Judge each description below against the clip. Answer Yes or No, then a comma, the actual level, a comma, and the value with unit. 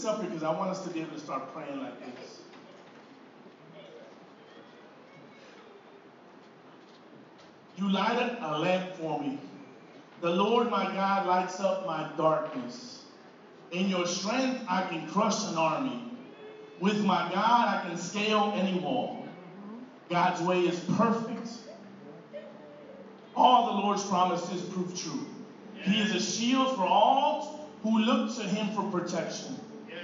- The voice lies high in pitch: Yes, high, 195 Hz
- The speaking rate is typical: No, slow, 130 wpm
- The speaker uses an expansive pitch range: No, average, 4.2 semitones